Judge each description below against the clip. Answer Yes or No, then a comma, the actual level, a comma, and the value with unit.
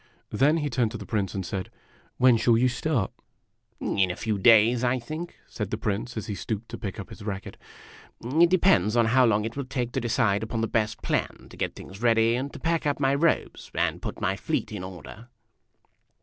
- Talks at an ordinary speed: No, fast, 220 wpm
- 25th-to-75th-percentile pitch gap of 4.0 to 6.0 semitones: No, average, 3.5 semitones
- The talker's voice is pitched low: Yes, low, 115 Hz